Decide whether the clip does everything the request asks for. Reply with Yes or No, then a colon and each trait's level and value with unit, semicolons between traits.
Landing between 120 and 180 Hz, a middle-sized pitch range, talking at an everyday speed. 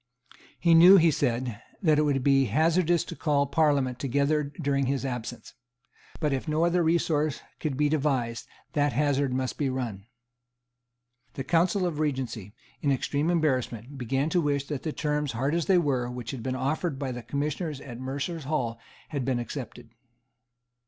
Yes: medium, 140 Hz; average, 3.3 semitones; average, 170 wpm